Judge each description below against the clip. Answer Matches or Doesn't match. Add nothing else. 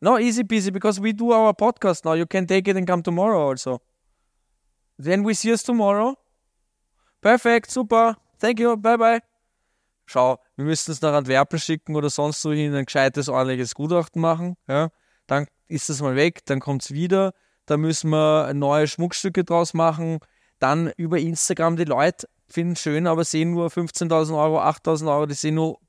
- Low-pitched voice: Doesn't match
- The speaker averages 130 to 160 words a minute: Doesn't match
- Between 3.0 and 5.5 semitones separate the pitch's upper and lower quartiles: Matches